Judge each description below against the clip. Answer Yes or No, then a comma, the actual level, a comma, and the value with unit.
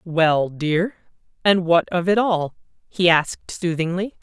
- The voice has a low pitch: No, medium, 175 Hz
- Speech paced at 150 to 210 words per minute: No, average, 140 wpm